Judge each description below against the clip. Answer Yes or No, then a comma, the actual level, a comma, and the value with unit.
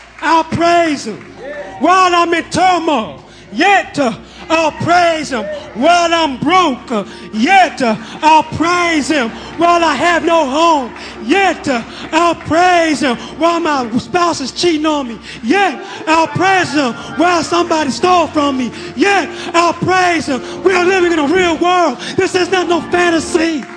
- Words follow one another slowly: No, average, 155 wpm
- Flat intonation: No, average, 3.1 semitones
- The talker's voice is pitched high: Yes, very high, 325 Hz